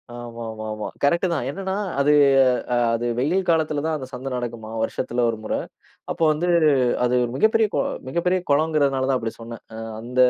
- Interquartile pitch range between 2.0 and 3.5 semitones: No, average, 5.3 semitones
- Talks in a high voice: No, low, 130 Hz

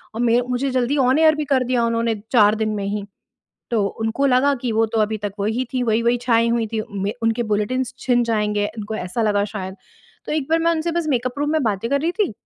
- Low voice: No, high, 235 Hz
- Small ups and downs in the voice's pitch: No, average, 3.6 semitones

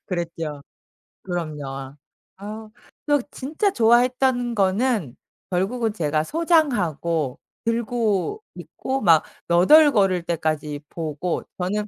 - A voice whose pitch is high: Yes, high, 195 Hz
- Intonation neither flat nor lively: No, wide, 7.0 semitones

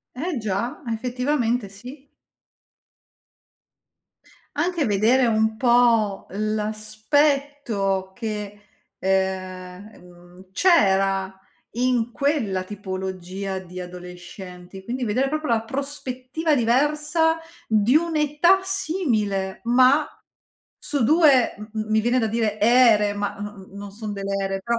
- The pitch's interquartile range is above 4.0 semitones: Yes, average, 5.2 semitones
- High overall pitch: Yes, high, 220 Hz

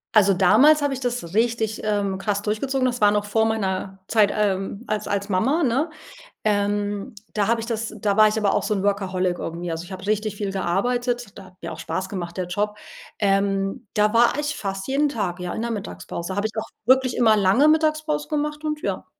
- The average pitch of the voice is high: Yes, high, 210 Hz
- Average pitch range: Yes, average, 3.7 semitones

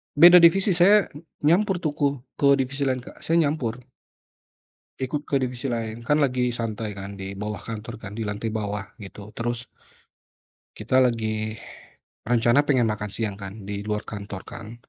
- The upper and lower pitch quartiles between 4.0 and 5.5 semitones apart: Yes, average, 4.6 semitones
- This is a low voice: Yes, low, 115 Hz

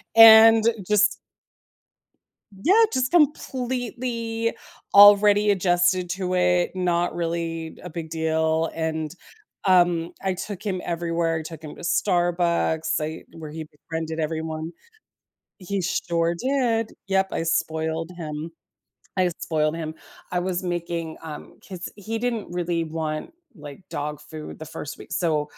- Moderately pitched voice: Yes, medium, 175 Hz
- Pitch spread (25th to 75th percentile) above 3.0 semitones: Yes, average, 3.5 semitones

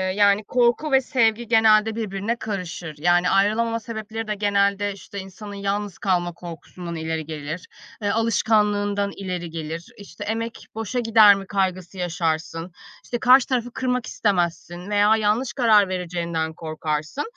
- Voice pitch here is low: No, high, 200 Hz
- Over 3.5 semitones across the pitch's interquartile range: Yes, average, 4.2 semitones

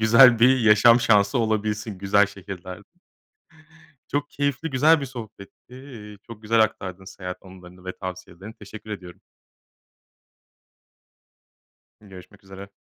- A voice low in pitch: Yes, low, 105 Hz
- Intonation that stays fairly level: No, average, 3.5 semitones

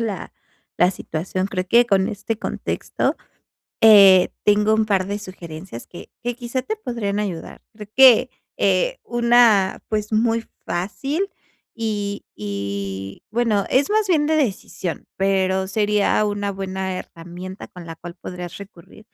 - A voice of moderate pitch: No, high, 205 Hz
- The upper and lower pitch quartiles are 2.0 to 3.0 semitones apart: No, average, 3.7 semitones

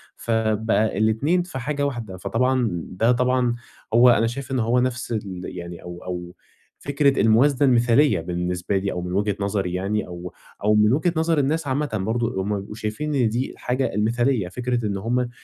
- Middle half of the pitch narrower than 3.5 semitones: No, average, 4.6 semitones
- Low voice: Yes, low, 115 Hz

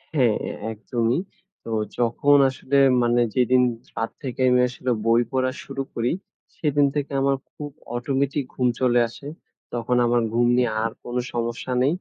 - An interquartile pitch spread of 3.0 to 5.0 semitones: No, narrow, 2.4 semitones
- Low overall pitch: Yes, low, 125 Hz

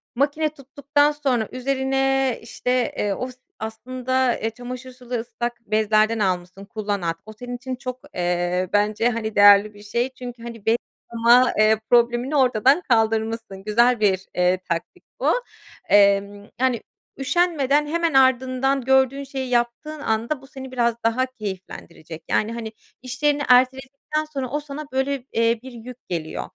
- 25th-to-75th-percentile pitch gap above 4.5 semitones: No, average, 3.5 semitones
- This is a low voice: No, high, 245 Hz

